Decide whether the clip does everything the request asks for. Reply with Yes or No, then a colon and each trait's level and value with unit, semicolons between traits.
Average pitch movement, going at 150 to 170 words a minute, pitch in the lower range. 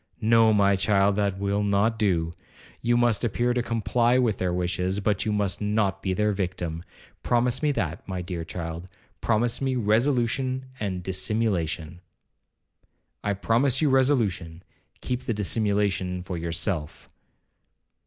No: average, 4.2 semitones; slow, 135 wpm; low, 100 Hz